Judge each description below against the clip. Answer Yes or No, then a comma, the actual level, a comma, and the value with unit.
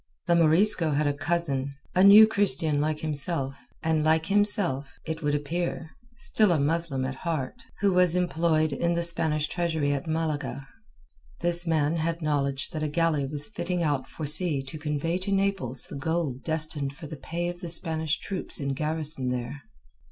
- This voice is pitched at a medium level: Yes, medium, 160 Hz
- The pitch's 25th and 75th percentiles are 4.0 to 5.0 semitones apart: No, average, 2.9 semitones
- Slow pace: No, average, 170 wpm